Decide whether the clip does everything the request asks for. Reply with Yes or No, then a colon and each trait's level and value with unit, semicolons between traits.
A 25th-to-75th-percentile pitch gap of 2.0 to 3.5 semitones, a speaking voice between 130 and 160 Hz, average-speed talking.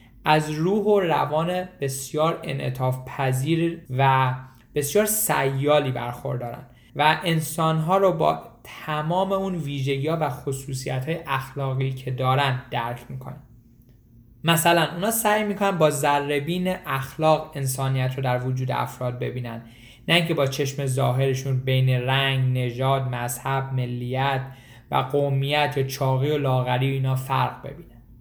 Yes: average, 3.2 semitones; low, 135 Hz; average, 130 wpm